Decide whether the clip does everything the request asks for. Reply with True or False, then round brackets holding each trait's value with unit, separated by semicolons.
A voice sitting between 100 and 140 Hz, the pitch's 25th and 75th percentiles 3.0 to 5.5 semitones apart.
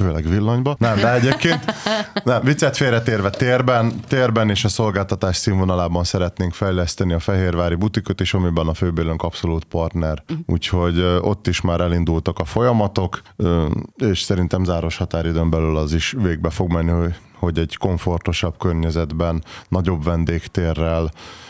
False (90 Hz; 4.4 semitones)